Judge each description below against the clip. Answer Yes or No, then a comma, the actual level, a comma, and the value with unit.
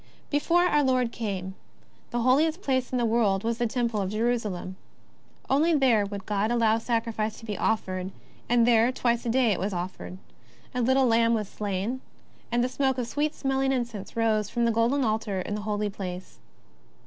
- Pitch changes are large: No, average, 3.4 semitones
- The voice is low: No, high, 230 Hz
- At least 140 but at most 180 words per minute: No, average, 190 wpm